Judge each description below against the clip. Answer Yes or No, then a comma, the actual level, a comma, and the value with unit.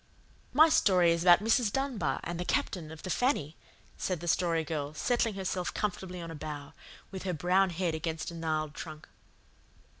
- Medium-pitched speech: Yes, medium, 175 Hz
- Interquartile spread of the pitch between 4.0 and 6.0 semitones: No, average, 3.3 semitones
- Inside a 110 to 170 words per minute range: No, average, 180 wpm